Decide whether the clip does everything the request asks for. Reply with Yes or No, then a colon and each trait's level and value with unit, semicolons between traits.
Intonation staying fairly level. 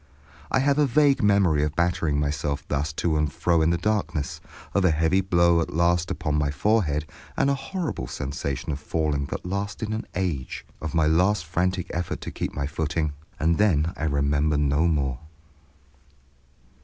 No: average, 4.2 semitones